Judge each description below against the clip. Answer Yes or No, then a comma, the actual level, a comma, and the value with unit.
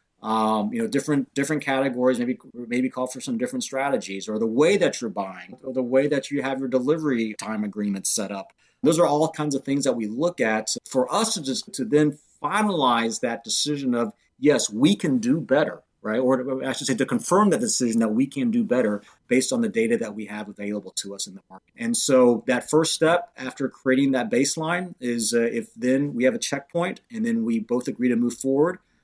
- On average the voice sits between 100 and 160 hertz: Yes, low, 135 Hz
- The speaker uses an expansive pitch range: Yes, wide, 6.4 semitones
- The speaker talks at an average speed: No, fast, 225 wpm